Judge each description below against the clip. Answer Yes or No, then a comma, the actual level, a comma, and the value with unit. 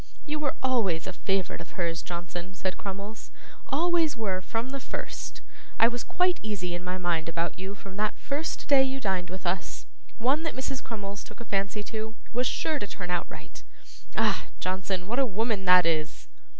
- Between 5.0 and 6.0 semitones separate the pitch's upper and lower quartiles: Yes, wide, 5.6 semitones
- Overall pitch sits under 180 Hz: No, high, 200 Hz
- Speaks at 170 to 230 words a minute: Yes, average, 190 wpm